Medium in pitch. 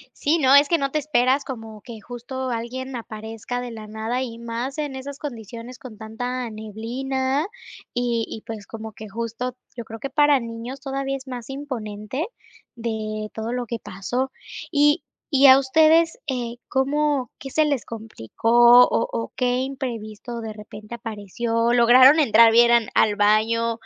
No: high, 240 Hz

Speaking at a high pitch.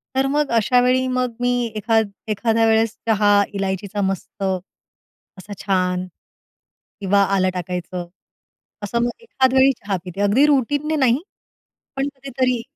Yes: high, 225 Hz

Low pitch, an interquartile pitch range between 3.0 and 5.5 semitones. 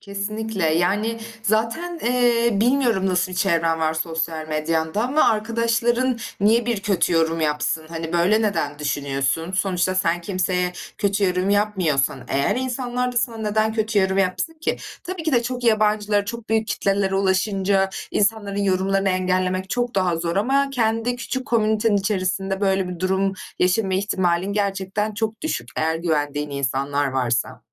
No: high, 195 Hz; average, 4.5 semitones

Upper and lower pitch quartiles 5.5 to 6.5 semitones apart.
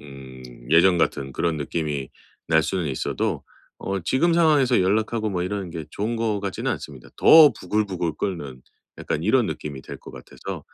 Yes: wide, 6.2 semitones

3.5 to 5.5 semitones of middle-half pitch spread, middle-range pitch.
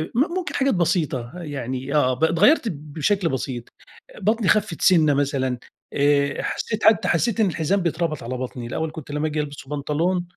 Yes: average, 4.7 semitones; medium, 155 Hz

